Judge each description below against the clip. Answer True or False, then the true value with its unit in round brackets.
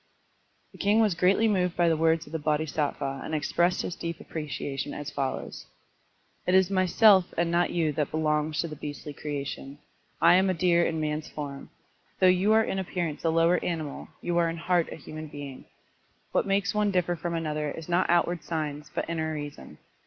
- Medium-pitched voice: True (165 Hz)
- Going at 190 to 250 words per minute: True (205 wpm)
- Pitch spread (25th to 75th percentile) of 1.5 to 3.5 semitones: True (2.9 semitones)